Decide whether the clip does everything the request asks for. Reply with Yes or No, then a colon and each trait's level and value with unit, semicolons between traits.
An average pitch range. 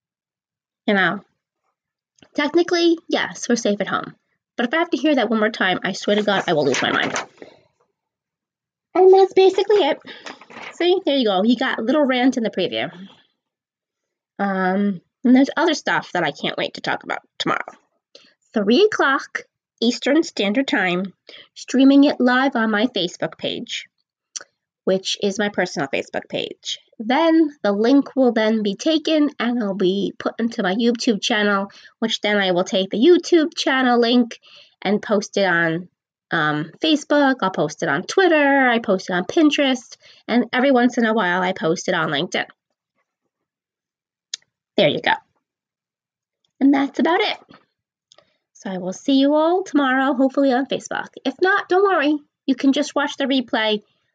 No: wide, 6.5 semitones